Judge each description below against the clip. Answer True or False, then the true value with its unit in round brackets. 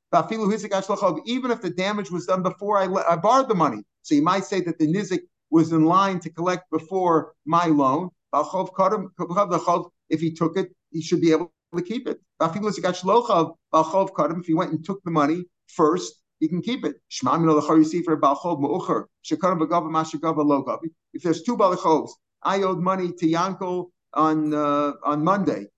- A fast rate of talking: False (150 wpm)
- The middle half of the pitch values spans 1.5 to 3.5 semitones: True (3.0 semitones)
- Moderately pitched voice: True (175 Hz)